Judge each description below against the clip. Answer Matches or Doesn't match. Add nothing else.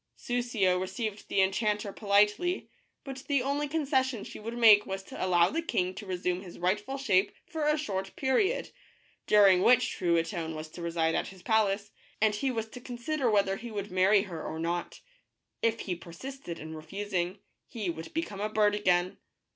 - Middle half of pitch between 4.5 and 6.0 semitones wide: Matches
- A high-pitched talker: Matches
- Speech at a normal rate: Matches